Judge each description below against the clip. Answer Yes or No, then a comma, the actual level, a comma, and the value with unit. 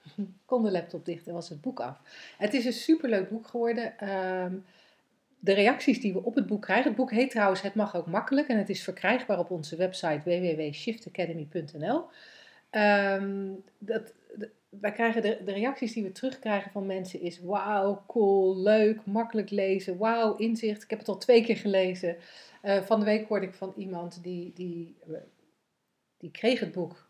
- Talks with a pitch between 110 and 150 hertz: No, high, 200 Hz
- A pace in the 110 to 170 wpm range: Yes, average, 165 wpm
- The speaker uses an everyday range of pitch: Yes, average, 3.5 semitones